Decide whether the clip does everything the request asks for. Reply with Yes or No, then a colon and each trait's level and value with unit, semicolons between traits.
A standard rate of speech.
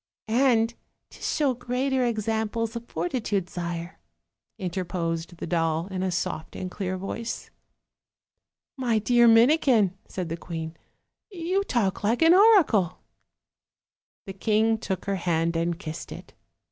No: slow, 130 wpm